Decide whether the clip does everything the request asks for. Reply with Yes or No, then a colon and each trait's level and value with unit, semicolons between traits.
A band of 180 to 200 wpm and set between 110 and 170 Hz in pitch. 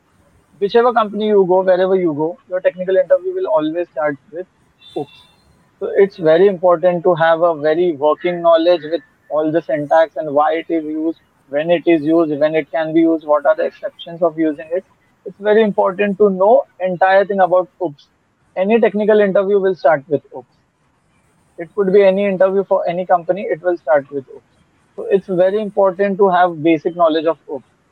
No: fast, 190 wpm; medium, 180 Hz